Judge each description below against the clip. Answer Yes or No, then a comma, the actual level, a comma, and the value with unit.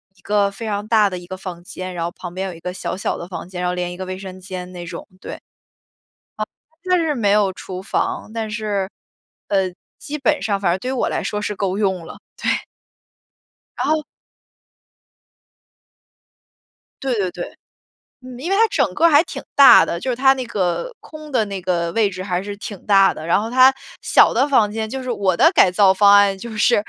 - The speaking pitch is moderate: No, high, 200 Hz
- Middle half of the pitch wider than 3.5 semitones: Yes, average, 4.5 semitones